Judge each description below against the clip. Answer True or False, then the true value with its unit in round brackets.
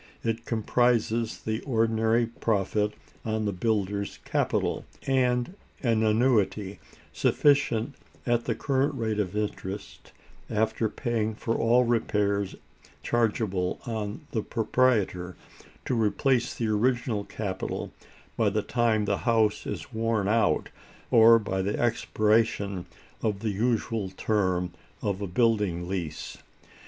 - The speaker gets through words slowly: True (120 wpm)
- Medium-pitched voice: False (110 Hz)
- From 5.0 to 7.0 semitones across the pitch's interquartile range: False (2.4 semitones)